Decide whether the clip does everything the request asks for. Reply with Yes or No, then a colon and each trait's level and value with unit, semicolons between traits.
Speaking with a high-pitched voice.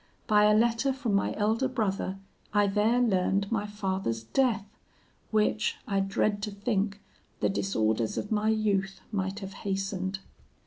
Yes: high, 205 Hz